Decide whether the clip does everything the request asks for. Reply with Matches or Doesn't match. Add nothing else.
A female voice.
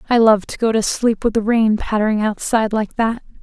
Matches